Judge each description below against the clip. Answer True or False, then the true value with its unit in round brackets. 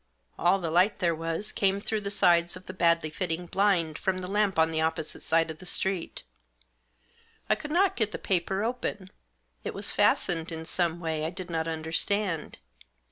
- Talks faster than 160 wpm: True (190 wpm)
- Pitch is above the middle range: False (175 Hz)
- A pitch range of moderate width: True (3.2 semitones)